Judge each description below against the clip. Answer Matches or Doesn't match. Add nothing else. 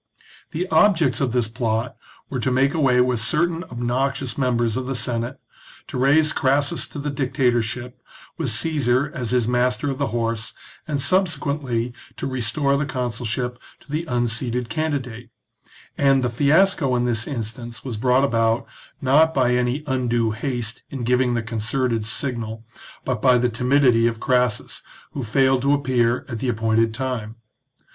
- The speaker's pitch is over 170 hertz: Doesn't match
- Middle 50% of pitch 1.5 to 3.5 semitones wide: Matches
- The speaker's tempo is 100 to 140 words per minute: Doesn't match